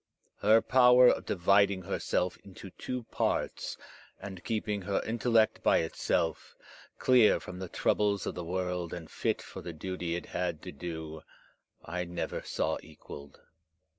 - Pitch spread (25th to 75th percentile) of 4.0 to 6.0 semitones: No, average, 3.3 semitones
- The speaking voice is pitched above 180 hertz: No, very low, 90 Hz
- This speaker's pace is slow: No, average, 145 wpm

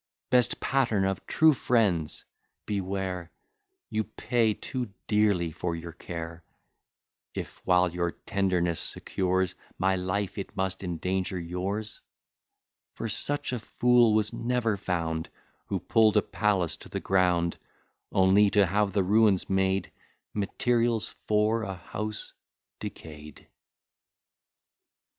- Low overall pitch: Yes, very low, 95 Hz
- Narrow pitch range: No, average, 3.2 semitones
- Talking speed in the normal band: No, slow, 115 wpm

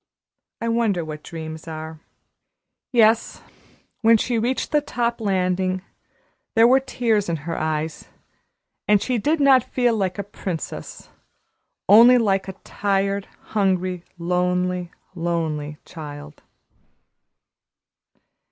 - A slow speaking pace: Yes, slow, 110 wpm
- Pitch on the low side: No, high, 190 Hz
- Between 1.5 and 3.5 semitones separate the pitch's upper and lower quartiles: No, wide, 5.4 semitones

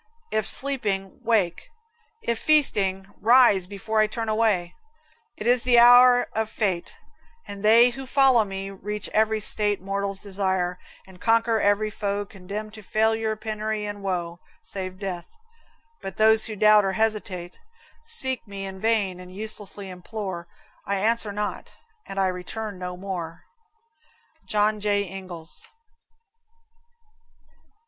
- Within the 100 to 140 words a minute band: Yes, slow, 135 wpm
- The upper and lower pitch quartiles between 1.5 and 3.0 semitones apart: Yes, narrow, 2.4 semitones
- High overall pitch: Yes, high, 205 Hz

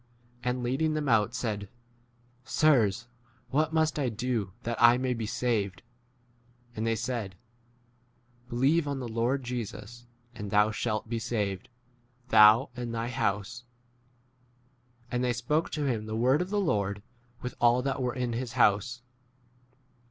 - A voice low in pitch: Yes, low, 120 Hz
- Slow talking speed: No, average, 160 wpm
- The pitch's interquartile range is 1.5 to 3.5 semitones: Yes, average, 2.9 semitones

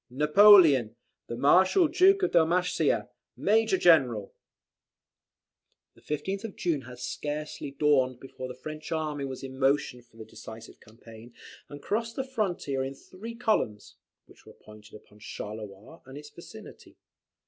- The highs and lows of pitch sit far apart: Yes, wide, 7.2 semitones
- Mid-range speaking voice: Yes, medium, 145 Hz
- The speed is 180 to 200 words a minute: No, average, 140 wpm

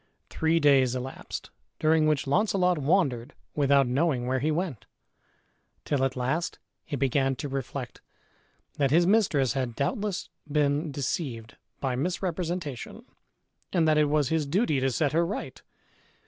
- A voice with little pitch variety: No, average, 3.8 semitones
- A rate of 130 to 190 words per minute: Yes, average, 140 wpm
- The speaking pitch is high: No, medium, 145 Hz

